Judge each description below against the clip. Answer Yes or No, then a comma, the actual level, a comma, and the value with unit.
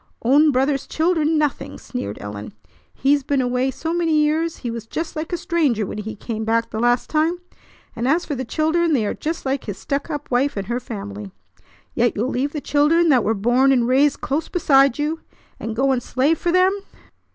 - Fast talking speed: Yes, fast, 210 wpm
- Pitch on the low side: No, very high, 275 Hz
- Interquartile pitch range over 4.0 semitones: Yes, average, 4.9 semitones